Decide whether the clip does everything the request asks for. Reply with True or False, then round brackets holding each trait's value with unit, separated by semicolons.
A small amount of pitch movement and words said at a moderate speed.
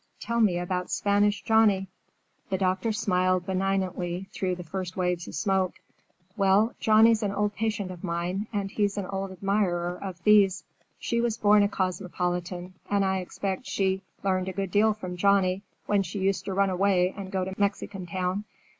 True (1.9 semitones; 175 wpm)